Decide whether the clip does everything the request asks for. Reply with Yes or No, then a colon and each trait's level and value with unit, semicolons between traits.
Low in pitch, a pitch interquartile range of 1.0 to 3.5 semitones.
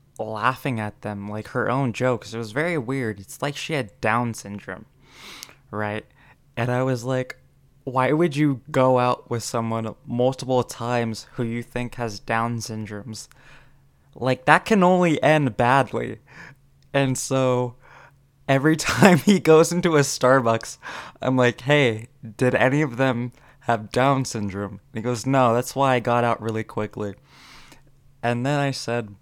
Yes: low, 125 Hz; average, 3.1 semitones